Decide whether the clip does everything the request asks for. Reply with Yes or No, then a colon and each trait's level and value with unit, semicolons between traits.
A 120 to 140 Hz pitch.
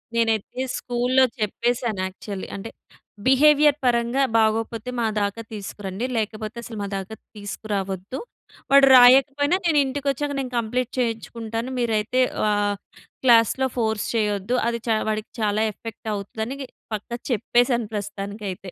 No: high, 225 Hz